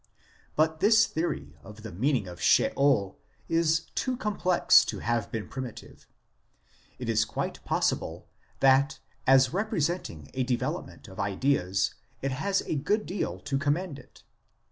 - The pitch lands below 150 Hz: Yes, medium, 140 Hz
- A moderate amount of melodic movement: No, wide, 7.1 semitones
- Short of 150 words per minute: Yes, average, 140 wpm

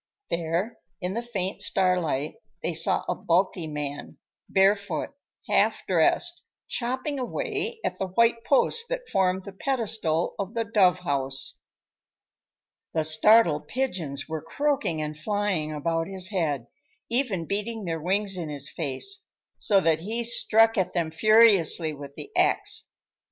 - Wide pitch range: Yes, wide, 6.2 semitones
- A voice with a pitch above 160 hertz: Yes, high, 190 Hz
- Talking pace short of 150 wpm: Yes, average, 140 wpm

